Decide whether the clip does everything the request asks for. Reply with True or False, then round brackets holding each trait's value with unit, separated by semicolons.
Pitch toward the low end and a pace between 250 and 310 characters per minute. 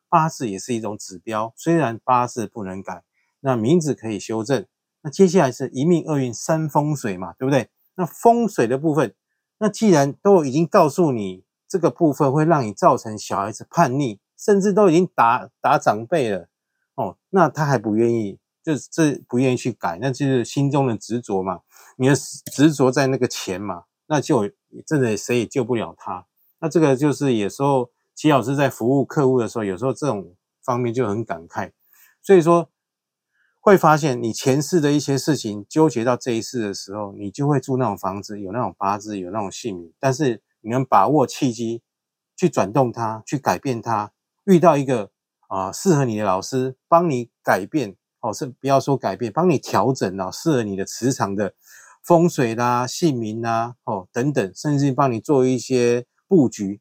True (130 Hz; 275 characters per minute)